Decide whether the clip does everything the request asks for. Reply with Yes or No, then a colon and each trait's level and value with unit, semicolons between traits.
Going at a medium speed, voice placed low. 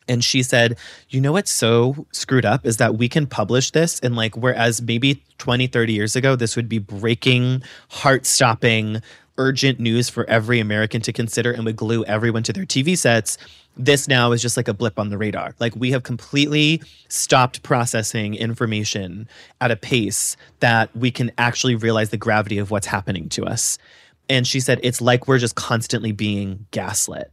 Yes: average, 190 wpm; low, 120 Hz